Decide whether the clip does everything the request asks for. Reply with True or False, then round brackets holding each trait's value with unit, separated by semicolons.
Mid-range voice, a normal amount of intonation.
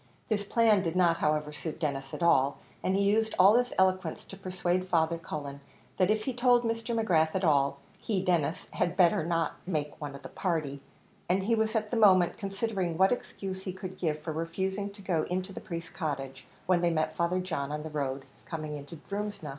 True (180 Hz; 4.0 semitones)